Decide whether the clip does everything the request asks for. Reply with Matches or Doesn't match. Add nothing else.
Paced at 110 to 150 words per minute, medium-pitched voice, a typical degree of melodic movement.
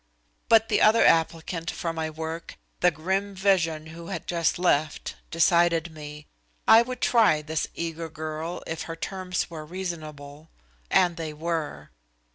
Doesn't match